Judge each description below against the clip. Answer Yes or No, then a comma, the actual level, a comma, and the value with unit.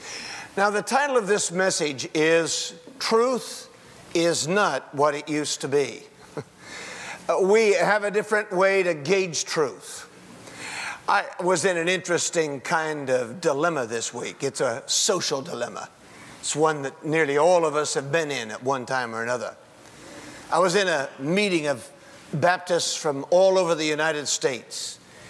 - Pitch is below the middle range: No, medium, 165 Hz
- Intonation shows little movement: No, average, 4.7 semitones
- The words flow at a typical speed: Yes, average, 155 wpm